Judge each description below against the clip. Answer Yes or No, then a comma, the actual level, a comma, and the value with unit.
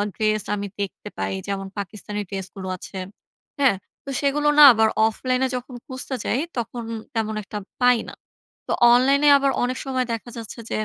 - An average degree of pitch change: Yes, average, 3.8 semitones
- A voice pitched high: Yes, high, 235 Hz